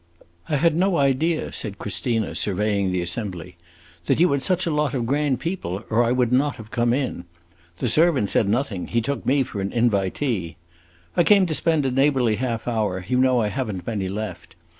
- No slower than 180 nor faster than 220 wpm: Yes, fast, 205 wpm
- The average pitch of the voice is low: Yes, low, 120 Hz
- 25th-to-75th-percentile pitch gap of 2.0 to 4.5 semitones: No, wide, 5.5 semitones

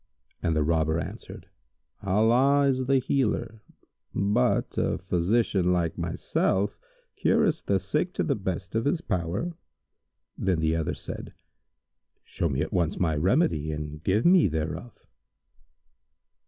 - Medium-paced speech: No, slow, 130 wpm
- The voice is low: Yes, very low, 95 Hz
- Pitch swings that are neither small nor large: No, wide, 6.8 semitones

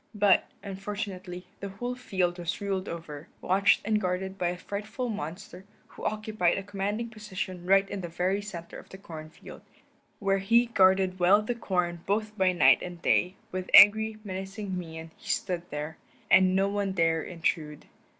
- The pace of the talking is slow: No, average, 170 wpm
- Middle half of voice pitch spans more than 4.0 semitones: No, narrow, 2.5 semitones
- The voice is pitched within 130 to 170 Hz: No, high, 190 Hz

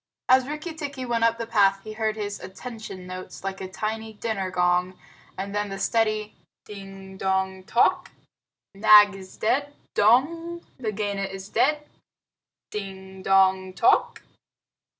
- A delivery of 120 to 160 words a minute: Yes, slow, 135 wpm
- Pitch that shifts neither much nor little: Yes, average, 3.2 semitones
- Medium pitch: No, high, 205 Hz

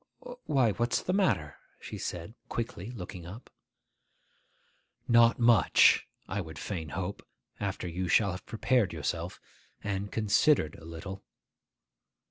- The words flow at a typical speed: No, slow, 120 wpm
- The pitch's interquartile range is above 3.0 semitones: Yes, average, 5.1 semitones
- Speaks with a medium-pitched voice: No, low, 100 Hz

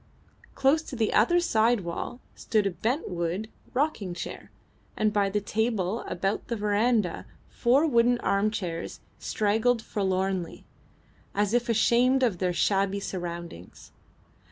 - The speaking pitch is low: No, high, 210 Hz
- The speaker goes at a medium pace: No, slow, 130 wpm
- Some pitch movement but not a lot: Yes, average, 4.0 semitones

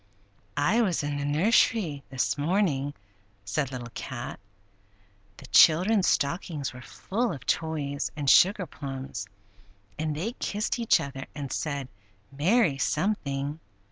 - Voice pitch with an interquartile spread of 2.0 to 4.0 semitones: No, average, 4.9 semitones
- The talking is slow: Yes, slow, 120 wpm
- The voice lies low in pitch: No, medium, 145 Hz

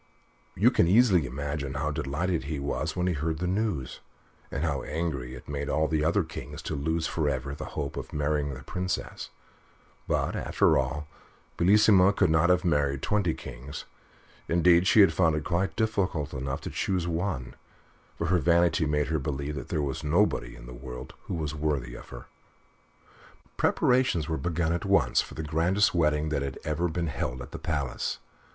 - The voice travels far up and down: No, average, 3.6 semitones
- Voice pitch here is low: Yes, very low, 80 Hz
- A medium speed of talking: Yes, average, 185 wpm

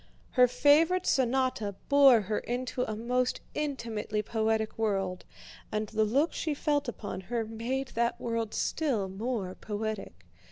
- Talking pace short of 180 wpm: Yes, slow, 135 wpm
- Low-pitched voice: No, high, 230 Hz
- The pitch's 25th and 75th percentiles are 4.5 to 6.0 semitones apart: No, average, 3.5 semitones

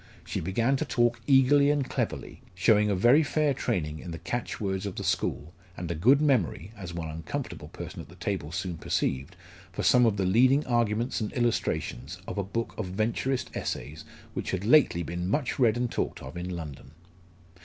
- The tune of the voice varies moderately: No, wide, 6.1 semitones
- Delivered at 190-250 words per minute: Yes, average, 195 wpm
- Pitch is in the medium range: No, low, 105 Hz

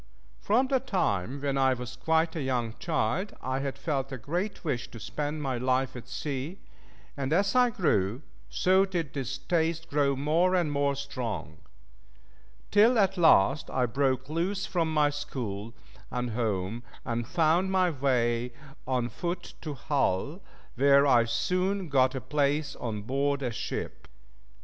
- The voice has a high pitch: No, medium, 140 Hz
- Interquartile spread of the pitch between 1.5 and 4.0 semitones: No, average, 5.0 semitones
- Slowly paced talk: No, average, 155 wpm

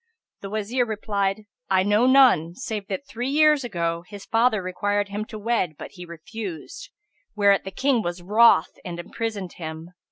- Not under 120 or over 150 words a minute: No, average, 165 wpm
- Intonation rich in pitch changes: No, average, 4.1 semitones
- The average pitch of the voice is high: Yes, high, 205 Hz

